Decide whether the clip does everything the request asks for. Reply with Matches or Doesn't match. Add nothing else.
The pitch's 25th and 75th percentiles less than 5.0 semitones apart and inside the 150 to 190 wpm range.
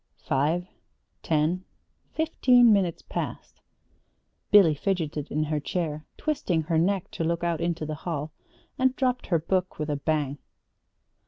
Doesn't match